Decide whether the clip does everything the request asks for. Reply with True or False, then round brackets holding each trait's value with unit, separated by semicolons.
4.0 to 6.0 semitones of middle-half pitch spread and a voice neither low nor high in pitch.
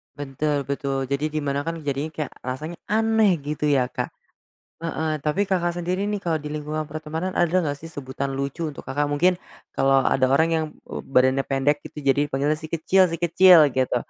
False (3.2 semitones; 150 Hz)